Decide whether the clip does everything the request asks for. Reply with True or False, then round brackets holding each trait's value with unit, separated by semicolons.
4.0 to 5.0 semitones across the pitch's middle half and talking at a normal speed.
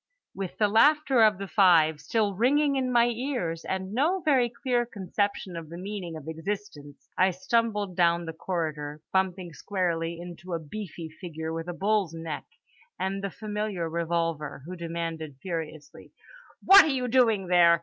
True (4.5 semitones; 160 wpm)